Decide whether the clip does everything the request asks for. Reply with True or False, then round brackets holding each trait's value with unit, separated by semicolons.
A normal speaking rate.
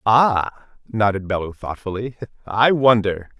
False (105 wpm)